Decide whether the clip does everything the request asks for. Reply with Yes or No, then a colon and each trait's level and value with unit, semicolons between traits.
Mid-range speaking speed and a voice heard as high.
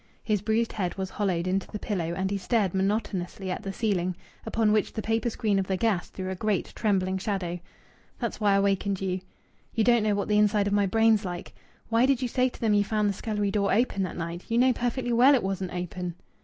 No: fast, 235 wpm; high, 200 Hz